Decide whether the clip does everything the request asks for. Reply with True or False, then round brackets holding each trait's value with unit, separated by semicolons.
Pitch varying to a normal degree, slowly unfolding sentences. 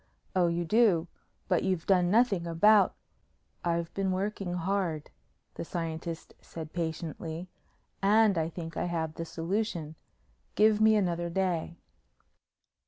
True (3.0 semitones; 130 wpm)